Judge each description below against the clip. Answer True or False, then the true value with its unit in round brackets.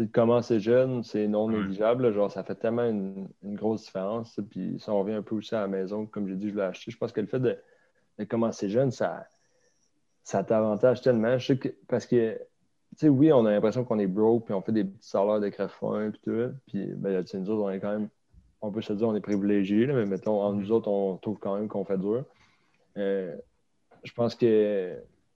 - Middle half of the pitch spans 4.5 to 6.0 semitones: False (2.4 semitones)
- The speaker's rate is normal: False (235 wpm)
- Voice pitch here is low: True (105 Hz)